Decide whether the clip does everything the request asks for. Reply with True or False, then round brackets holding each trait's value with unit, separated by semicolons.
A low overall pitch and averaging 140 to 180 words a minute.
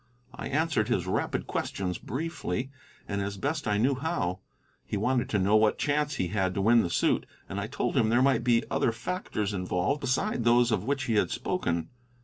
False (115 Hz; 200 wpm)